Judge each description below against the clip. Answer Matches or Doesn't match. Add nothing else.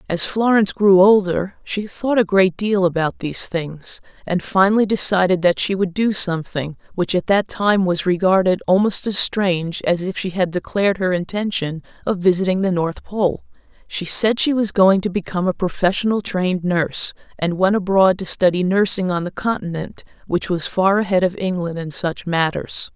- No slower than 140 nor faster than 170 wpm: Doesn't match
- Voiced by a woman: Matches